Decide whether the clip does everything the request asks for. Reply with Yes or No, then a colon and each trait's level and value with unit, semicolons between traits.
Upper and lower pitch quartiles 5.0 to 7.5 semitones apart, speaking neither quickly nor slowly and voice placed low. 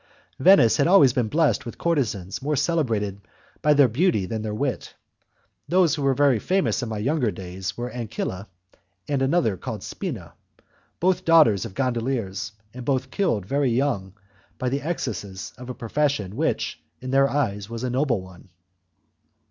Yes: wide, 5.4 semitones; average, 165 wpm; low, 125 Hz